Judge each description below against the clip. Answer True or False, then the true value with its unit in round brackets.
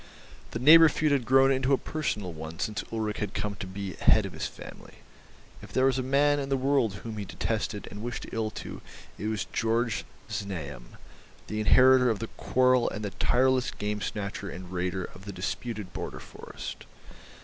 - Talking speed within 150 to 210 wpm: True (190 wpm)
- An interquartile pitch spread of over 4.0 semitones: True (4.5 semitones)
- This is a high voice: False (110 Hz)